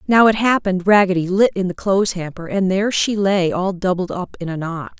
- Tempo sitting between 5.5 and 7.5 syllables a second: Yes, 5.7 syllables/s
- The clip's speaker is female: Yes, female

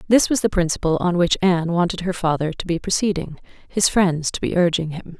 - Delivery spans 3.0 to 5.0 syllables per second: No, 5.8 syllables/s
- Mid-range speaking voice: Yes, medium, 175 Hz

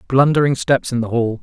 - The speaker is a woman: No, male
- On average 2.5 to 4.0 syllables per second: No, 5.5 syllables/s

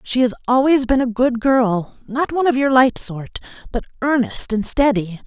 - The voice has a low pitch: No, high, 245 Hz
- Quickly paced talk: No, average, 195 wpm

